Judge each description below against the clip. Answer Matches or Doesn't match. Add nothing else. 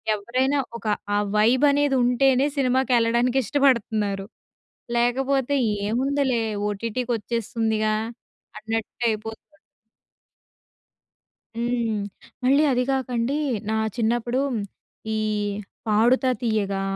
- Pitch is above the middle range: Matches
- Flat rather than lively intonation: Doesn't match